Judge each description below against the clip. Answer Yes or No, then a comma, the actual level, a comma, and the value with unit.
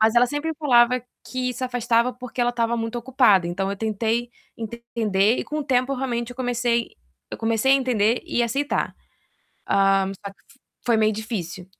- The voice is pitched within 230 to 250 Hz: Yes, high, 235 Hz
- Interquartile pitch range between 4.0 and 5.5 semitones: No, narrow, 2.5 semitones